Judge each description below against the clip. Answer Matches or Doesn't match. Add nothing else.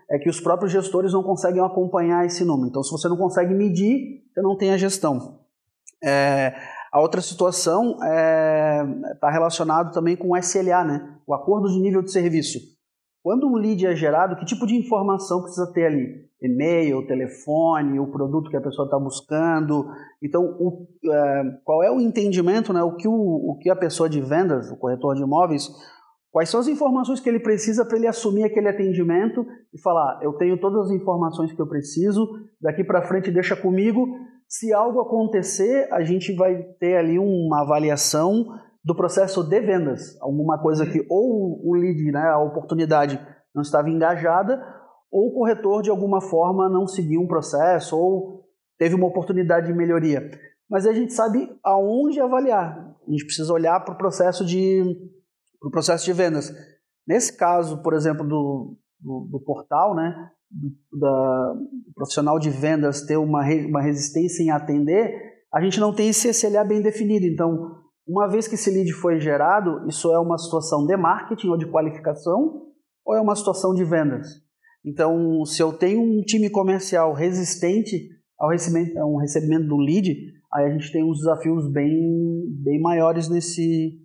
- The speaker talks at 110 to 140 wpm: Doesn't match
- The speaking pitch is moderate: Matches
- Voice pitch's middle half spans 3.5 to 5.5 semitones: Matches